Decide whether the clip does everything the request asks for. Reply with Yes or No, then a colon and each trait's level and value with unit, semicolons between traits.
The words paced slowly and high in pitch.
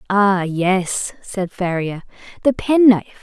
Yes: slow, 110 wpm; high, 195 Hz